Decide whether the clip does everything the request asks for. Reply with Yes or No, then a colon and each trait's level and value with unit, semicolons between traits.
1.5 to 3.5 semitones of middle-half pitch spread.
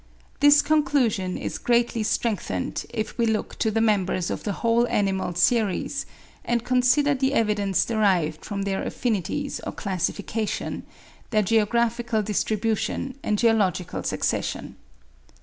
Yes: average, 3.1 semitones